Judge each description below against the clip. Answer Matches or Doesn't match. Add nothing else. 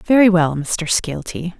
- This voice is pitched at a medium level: Matches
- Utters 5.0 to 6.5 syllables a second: Doesn't match